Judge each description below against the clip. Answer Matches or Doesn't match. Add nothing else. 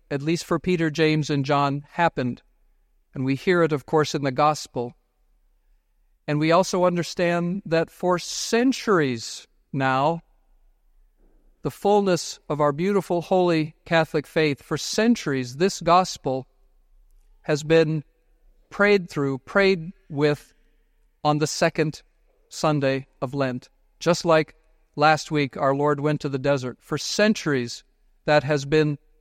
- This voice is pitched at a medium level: Matches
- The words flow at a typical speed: Doesn't match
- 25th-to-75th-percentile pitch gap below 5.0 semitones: Matches